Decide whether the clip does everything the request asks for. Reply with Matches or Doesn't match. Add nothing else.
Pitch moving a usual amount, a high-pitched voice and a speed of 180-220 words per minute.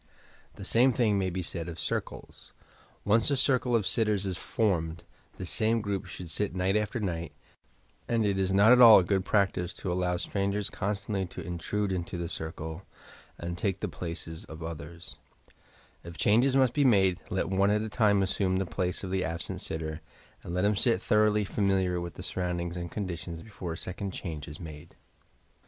Doesn't match